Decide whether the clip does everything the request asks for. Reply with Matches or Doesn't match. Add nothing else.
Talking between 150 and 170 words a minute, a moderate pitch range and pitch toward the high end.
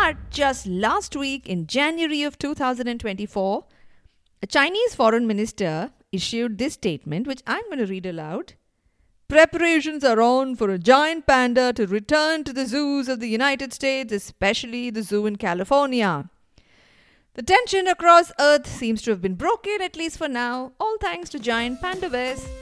Doesn't match